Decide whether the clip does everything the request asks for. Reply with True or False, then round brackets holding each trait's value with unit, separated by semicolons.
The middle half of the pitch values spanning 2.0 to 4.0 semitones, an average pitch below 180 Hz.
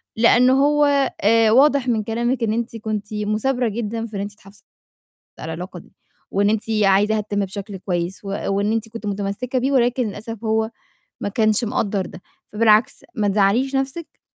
False (2.7 semitones; 220 Hz)